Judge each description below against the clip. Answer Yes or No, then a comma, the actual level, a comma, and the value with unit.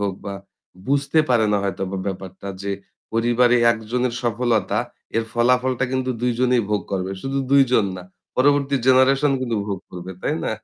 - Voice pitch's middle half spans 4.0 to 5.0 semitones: Yes, average, 4.4 semitones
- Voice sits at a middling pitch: No, low, 120 Hz